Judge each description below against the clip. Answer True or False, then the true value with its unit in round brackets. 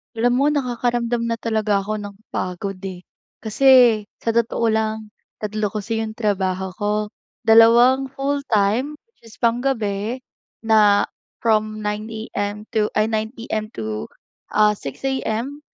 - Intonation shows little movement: True (2.3 semitones)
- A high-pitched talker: True (220 Hz)